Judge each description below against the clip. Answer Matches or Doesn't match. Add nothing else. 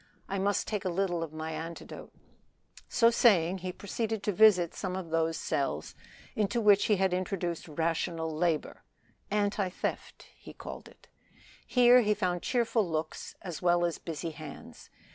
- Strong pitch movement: Doesn't match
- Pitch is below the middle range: Doesn't match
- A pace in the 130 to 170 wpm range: Matches